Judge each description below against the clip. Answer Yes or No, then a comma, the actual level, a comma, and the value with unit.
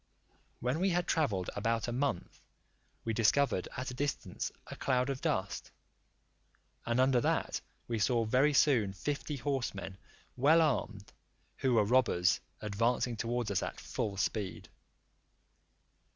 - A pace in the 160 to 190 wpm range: No, slow, 135 wpm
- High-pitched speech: No, low, 120 Hz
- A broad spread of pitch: No, average, 4.6 semitones